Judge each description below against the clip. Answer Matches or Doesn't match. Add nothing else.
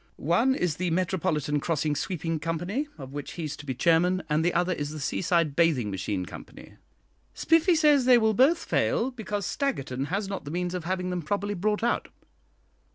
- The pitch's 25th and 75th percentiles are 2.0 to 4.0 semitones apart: Doesn't match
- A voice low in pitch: Doesn't match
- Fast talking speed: Doesn't match